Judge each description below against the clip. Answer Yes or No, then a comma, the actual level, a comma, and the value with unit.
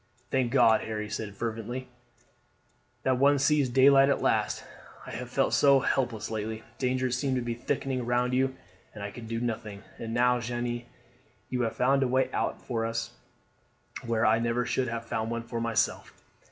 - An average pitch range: No, narrow, 2.3 semitones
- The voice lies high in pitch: No, low, 120 Hz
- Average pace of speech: Yes, average, 180 wpm